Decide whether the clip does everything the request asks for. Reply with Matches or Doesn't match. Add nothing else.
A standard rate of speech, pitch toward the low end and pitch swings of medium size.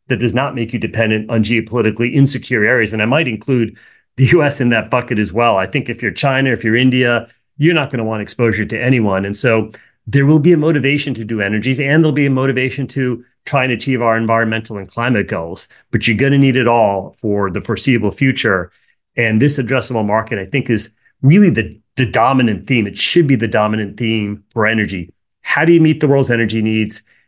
Doesn't match